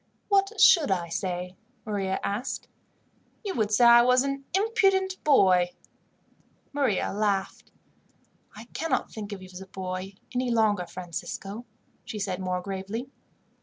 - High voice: Yes, high, 205 Hz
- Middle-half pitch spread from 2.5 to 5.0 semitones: No, wide, 5.5 semitones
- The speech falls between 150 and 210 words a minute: No, slow, 135 wpm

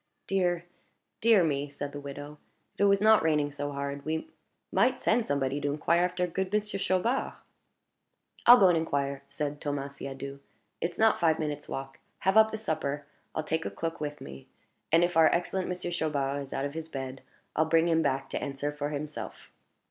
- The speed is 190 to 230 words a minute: Yes, average, 195 wpm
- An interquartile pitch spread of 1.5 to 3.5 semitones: No, average, 3.9 semitones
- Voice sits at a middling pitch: Yes, medium, 155 Hz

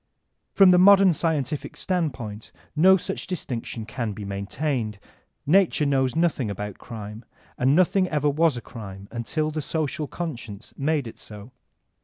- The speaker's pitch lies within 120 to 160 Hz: Yes, medium, 140 Hz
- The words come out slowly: No, average, 145 wpm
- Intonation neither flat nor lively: No, wide, 6.7 semitones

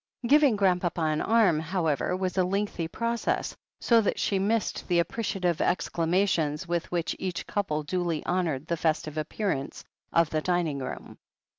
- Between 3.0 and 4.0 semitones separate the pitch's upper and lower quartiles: Yes, average, 3.6 semitones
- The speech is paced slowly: No, average, 155 wpm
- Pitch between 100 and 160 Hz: No, medium, 175 Hz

